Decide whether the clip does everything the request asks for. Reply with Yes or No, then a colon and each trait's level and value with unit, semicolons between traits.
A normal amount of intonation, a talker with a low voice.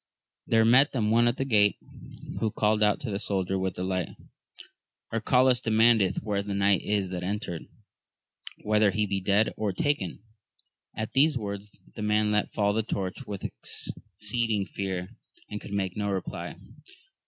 No: narrow, 2.2 semitones; low, 105 Hz